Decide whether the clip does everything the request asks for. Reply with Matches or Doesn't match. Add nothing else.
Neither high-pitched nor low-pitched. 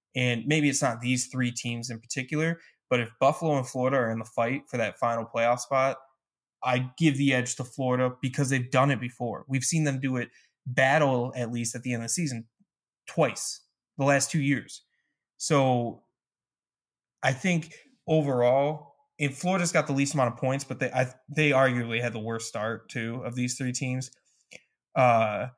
Doesn't match